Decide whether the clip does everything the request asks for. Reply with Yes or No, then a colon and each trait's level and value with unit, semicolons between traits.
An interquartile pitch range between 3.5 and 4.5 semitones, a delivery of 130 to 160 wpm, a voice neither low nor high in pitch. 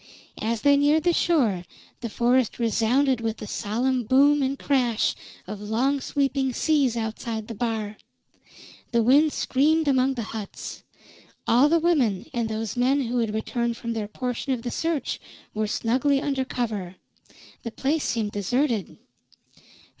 No: average, 3.9 semitones; average, 150 wpm; high, 245 Hz